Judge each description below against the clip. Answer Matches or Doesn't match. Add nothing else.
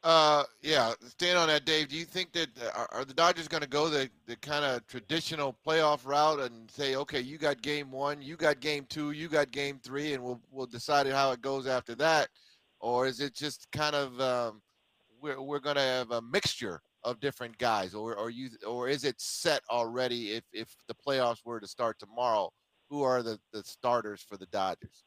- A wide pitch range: Doesn't match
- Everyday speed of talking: Doesn't match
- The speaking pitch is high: Doesn't match